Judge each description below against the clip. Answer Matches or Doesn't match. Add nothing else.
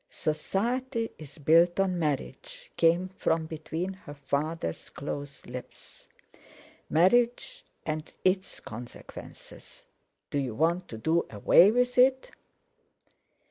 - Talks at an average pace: Doesn't match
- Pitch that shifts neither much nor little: Matches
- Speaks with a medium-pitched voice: Matches